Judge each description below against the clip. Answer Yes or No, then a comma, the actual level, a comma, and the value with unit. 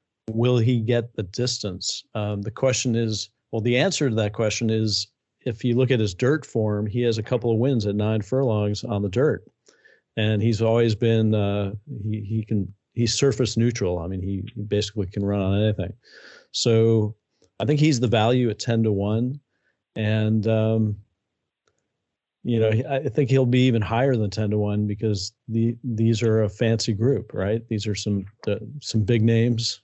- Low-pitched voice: Yes, low, 110 Hz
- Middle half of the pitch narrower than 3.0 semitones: Yes, narrow, 2.4 semitones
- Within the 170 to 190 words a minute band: Yes, average, 185 wpm